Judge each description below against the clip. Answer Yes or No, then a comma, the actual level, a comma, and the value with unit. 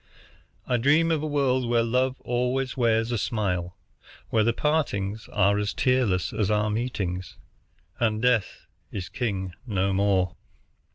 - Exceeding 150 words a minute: No, average, 145 wpm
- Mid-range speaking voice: No, low, 115 Hz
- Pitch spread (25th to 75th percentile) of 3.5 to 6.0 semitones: Yes, average, 4.2 semitones